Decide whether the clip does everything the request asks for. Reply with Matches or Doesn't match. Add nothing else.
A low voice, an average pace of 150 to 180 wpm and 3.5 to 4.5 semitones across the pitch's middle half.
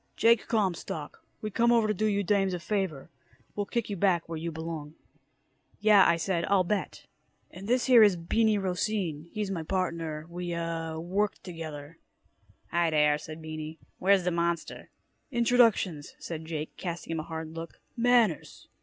Doesn't match